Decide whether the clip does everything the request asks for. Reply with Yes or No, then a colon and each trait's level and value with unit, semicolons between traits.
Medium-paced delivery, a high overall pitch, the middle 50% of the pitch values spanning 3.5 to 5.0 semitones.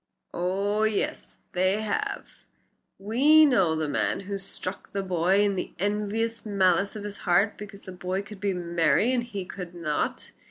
No: average, 165 wpm; high, 195 Hz; narrow, 2.5 semitones